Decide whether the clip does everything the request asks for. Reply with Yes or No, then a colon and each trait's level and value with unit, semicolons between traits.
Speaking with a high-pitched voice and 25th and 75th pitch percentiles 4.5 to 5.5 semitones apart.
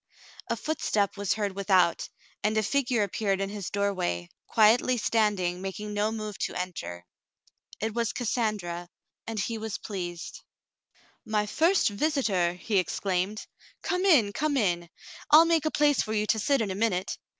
No: high, 210 Hz; average, 3.4 semitones